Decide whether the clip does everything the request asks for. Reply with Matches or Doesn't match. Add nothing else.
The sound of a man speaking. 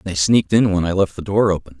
Matches